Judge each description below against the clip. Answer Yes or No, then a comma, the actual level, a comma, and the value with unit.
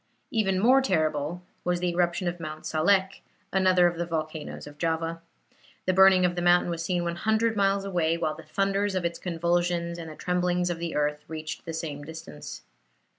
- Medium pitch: Yes, medium, 175 Hz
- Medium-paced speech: Yes, average, 185 wpm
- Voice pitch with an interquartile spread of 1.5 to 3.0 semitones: Yes, narrow, 2.4 semitones